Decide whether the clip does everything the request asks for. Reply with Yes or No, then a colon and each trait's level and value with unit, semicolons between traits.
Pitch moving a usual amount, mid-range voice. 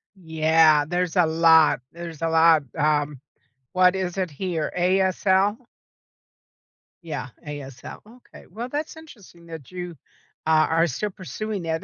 Yes: average, 3.0 semitones; medium, 170 Hz